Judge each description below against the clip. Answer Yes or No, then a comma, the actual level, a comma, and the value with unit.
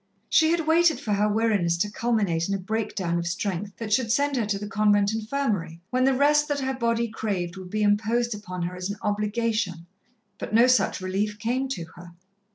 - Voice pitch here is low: No, high, 210 Hz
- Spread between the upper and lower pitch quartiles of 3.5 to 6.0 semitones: Yes, average, 3.8 semitones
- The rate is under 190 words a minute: No, fast, 205 wpm